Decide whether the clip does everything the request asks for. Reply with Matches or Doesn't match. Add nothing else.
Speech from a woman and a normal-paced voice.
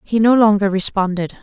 Matches